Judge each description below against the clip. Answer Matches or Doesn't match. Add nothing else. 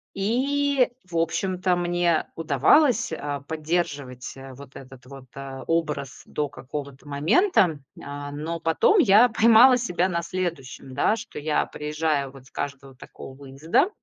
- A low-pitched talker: Doesn't match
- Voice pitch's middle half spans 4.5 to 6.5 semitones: Matches